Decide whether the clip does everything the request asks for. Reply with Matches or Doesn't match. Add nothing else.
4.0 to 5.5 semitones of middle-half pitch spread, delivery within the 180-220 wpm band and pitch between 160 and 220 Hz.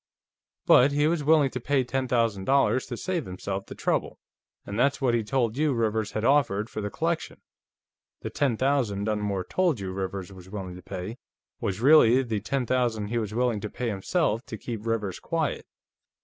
Doesn't match